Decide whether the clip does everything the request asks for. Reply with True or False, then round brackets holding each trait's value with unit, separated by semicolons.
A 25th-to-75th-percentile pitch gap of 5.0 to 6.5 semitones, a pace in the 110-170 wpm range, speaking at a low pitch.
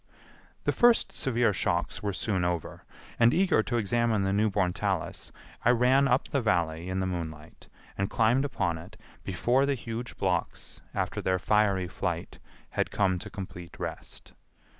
False (4.5 semitones; 160 wpm; 105 Hz)